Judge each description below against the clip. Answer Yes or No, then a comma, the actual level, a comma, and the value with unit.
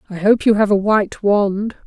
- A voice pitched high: Yes, high, 205 Hz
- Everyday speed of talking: No, fast, 225 wpm